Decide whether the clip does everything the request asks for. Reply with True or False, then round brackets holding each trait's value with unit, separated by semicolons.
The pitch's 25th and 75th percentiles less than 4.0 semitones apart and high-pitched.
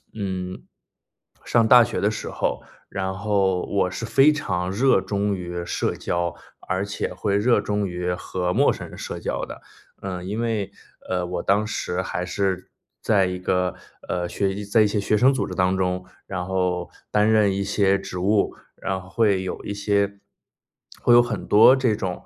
False (2.4 semitones; 100 Hz)